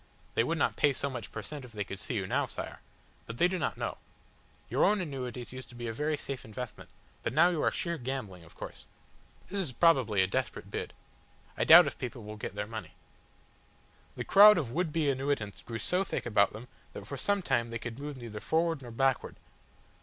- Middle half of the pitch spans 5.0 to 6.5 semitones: Yes, wide, 5.4 semitones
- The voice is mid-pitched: No, low, 125 Hz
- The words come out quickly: Yes, fast, 220 wpm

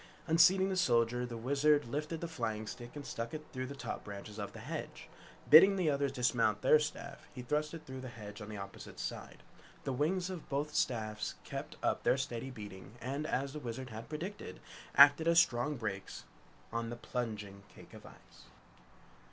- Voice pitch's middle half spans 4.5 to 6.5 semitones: Yes, average, 4.9 semitones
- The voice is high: No, low, 130 Hz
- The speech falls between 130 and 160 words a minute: No, average, 195 wpm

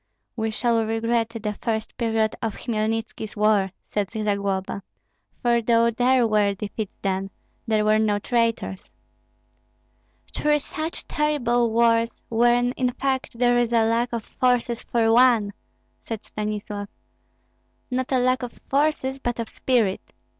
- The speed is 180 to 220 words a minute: No, slow, 135 wpm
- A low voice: No, high, 230 Hz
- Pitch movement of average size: No, narrow, 2.2 semitones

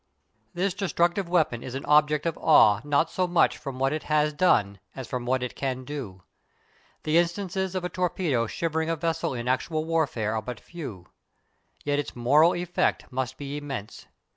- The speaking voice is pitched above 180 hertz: No, medium, 150 Hz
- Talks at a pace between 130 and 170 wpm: No, average, 180 wpm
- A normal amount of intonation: Yes, average, 4.9 semitones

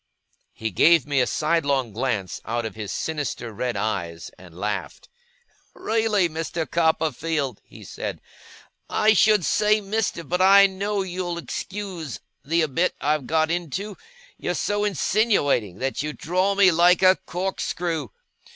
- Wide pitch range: Yes, wide, 6.5 semitones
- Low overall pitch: No, medium, 165 Hz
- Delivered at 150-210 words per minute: No, average, 140 wpm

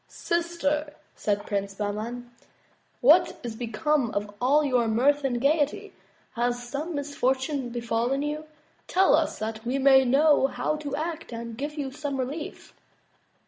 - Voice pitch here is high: Yes, very high, 270 Hz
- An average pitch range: Yes, average, 4.0 semitones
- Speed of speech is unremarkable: Yes, average, 145 wpm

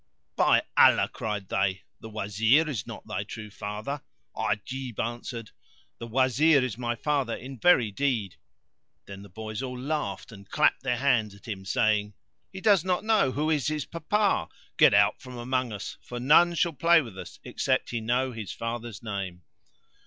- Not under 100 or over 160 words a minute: No, average, 175 wpm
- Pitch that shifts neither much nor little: Yes, average, 5.0 semitones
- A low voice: Yes, low, 120 Hz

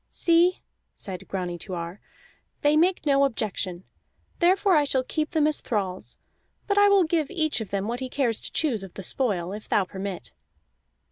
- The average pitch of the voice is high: Yes, very high, 255 Hz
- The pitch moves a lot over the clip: Yes, wide, 8.5 semitones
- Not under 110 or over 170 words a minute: No, average, 185 wpm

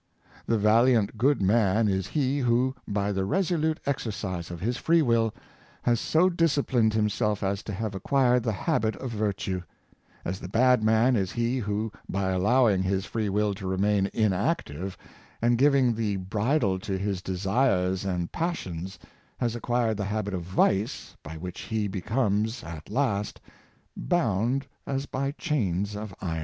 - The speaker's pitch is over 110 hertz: No, low, 105 Hz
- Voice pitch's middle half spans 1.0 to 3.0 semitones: No, average, 4.3 semitones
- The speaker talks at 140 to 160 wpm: Yes, average, 155 wpm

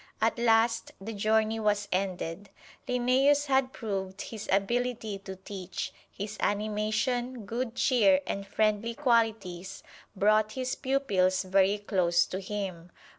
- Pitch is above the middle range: Yes, high, 215 Hz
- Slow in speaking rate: Yes, slow, 125 wpm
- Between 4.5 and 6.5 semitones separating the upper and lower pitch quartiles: No, average, 3.4 semitones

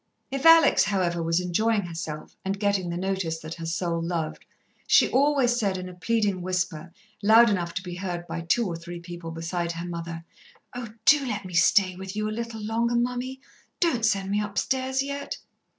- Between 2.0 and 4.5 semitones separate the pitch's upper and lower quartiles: No, average, 5.1 semitones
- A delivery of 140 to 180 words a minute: No, average, 190 wpm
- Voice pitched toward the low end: No, high, 190 Hz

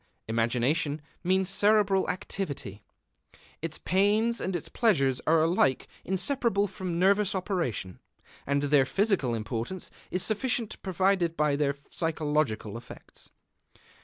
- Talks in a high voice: No, medium, 170 Hz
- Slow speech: Yes, slow, 110 wpm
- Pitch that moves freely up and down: Yes, wide, 5.8 semitones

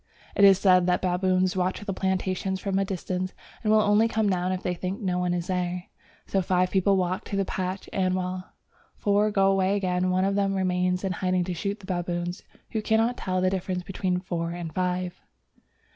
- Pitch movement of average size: No, narrow, 1.3 semitones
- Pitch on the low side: No, medium, 185 Hz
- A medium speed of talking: No, fast, 210 wpm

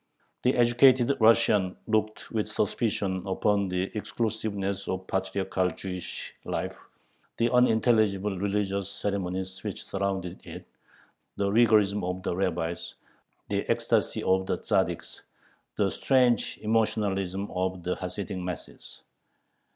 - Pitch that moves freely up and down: No, average, 2.7 semitones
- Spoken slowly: Yes, slow, 110 wpm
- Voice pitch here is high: No, low, 100 Hz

